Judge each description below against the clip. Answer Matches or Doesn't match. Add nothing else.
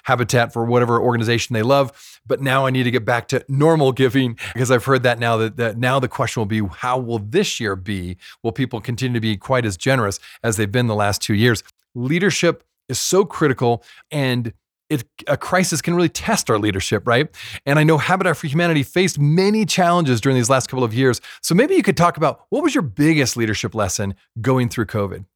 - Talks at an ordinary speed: Doesn't match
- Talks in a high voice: Doesn't match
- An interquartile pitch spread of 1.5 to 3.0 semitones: Doesn't match